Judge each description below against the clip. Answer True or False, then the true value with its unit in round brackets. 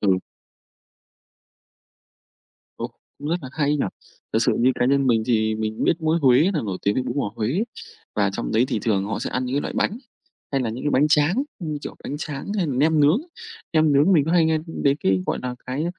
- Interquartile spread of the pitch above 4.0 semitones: True (4.9 semitones)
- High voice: False (140 Hz)